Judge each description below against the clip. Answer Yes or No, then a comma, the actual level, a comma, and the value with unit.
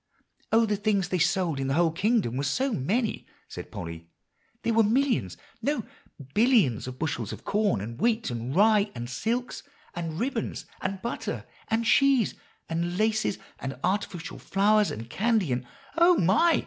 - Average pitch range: No, wide, 8.1 semitones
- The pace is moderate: Yes, average, 160 wpm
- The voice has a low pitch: No, high, 200 Hz